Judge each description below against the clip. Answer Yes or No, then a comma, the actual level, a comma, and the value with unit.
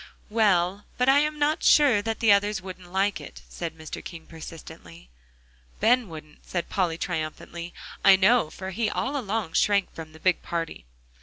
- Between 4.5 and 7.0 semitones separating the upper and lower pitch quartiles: Yes, average, 5.1 semitones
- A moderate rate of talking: Yes, average, 170 wpm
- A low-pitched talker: No, high, 190 Hz